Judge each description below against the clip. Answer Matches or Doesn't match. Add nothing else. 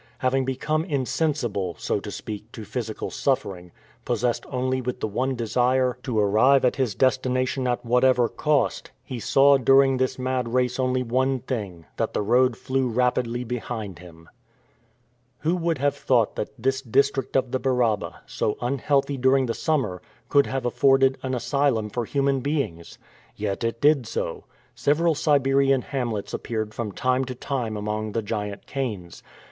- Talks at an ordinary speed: Matches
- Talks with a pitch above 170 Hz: Doesn't match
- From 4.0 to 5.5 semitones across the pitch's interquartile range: Doesn't match